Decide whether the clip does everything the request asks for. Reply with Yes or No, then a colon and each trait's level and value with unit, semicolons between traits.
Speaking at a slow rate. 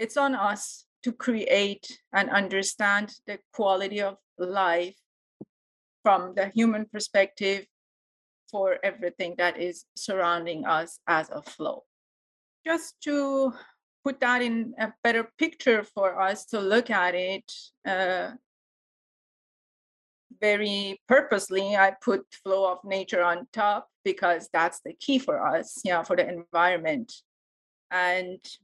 Yes: slow, 130 wpm